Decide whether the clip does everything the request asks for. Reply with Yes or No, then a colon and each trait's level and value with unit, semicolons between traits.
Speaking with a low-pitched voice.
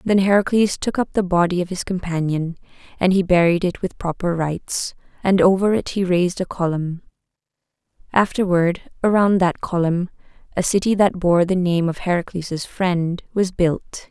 No: medium, 180 Hz